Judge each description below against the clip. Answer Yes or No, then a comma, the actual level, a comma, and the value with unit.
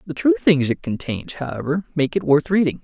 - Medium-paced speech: No, fast, 210 wpm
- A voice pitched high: No, medium, 155 Hz